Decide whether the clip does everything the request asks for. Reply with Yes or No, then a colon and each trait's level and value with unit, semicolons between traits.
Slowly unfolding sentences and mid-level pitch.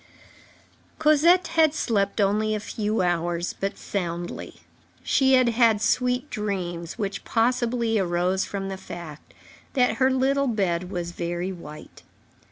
No: slow, 130 wpm; high, 205 Hz